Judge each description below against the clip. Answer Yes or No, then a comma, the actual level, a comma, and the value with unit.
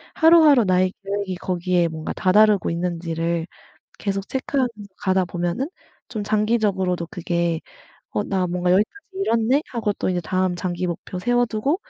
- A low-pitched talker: No, high, 190 Hz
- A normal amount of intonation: Yes, average, 4.0 semitones